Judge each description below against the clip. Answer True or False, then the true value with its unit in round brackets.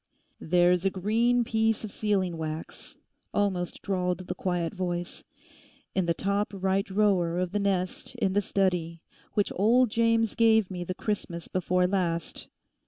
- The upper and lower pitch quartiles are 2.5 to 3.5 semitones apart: True (2.9 semitones)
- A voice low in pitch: False (190 Hz)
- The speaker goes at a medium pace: True (150 wpm)